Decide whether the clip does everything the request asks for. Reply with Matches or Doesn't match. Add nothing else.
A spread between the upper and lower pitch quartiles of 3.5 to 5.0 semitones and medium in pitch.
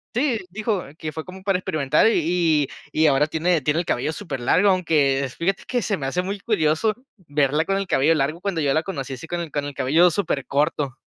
Matches